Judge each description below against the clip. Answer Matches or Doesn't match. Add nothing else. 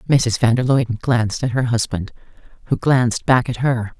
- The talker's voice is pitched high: Doesn't match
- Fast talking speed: Doesn't match